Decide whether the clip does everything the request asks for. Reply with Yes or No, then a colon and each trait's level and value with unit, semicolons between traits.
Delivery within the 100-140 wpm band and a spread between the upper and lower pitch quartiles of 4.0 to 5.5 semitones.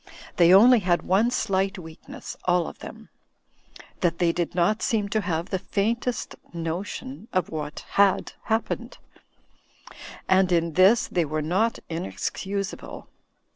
No: slow, 135 wpm; average, 3.6 semitones